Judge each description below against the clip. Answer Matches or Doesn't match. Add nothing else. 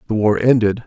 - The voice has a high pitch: Doesn't match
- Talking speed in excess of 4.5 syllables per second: Matches